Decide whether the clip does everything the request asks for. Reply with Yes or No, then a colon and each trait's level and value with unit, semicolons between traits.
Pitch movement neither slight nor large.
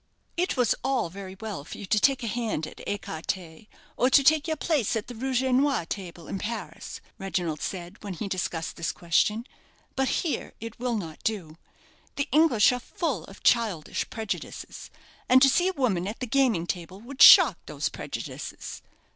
No: wide, 6.0 semitones